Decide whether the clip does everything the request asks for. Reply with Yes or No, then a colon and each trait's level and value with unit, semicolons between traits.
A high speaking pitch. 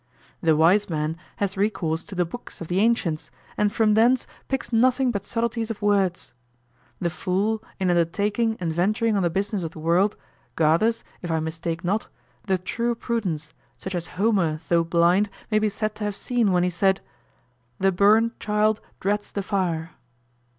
Yes: high, 195 Hz